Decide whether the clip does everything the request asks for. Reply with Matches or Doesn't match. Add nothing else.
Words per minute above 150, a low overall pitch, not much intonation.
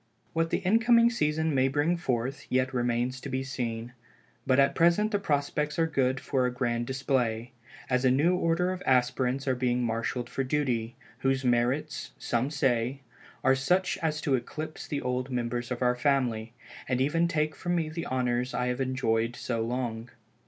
Doesn't match